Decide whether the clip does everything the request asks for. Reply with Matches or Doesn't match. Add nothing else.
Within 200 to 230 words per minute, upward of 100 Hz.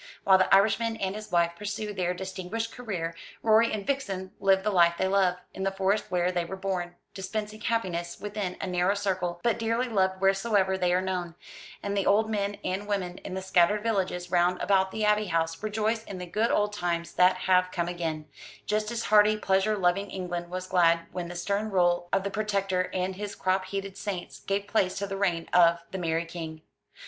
Matches